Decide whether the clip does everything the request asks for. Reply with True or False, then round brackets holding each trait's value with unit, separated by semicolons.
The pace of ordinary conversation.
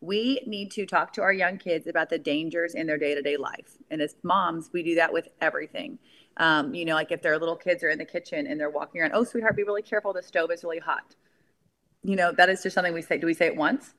False (275 wpm)